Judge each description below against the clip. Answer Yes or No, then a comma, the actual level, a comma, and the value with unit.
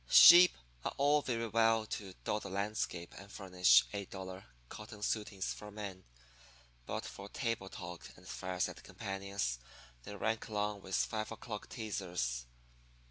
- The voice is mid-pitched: No, low, 100 Hz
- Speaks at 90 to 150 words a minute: Yes, average, 140 wpm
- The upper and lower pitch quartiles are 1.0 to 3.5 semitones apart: Yes, average, 2.7 semitones